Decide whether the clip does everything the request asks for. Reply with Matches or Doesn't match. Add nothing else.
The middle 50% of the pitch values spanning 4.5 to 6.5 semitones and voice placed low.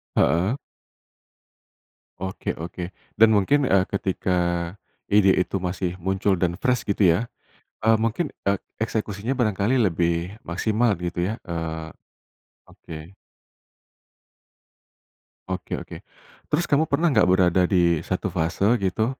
Doesn't match